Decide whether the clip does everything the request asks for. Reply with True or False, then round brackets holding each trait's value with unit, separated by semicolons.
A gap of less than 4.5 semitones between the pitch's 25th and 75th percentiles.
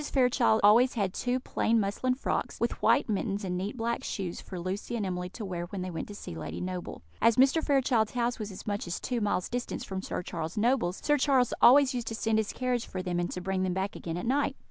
False (4.9 semitones)